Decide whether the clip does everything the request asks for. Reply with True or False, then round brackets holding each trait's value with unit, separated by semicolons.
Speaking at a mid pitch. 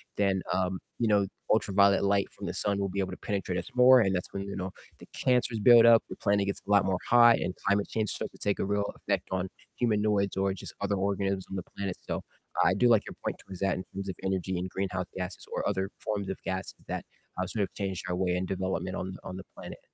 False (100 Hz)